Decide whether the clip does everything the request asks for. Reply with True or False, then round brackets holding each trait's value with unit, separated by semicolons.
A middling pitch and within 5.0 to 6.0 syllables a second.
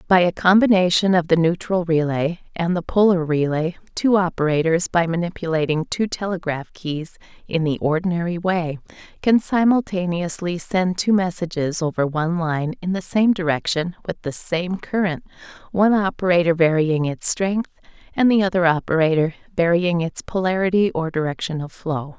True (175 Hz; 5.1 syllables/s)